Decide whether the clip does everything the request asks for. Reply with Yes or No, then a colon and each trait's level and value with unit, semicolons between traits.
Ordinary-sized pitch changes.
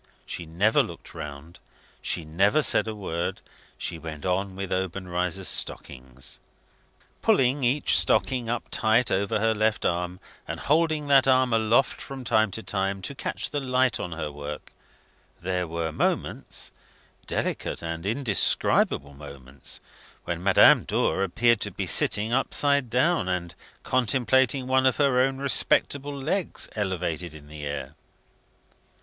No: wide, 7.2 semitones